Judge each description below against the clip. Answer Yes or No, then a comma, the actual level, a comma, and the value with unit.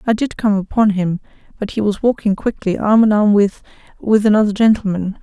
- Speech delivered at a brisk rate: No, average, 185 wpm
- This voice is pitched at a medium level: No, high, 205 Hz